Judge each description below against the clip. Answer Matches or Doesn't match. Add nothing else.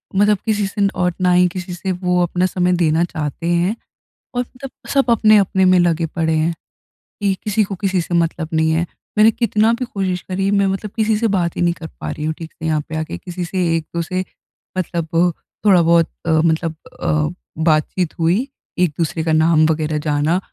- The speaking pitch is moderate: Matches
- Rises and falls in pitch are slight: Doesn't match